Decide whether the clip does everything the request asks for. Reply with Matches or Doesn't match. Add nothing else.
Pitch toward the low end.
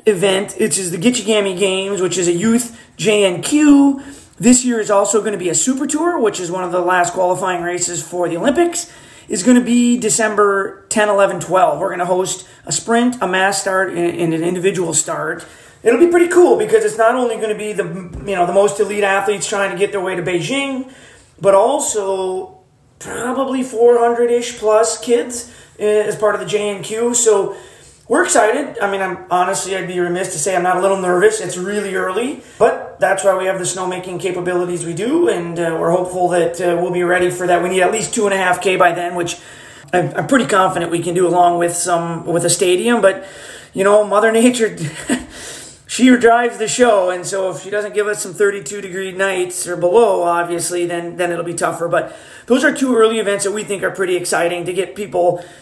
Doesn't match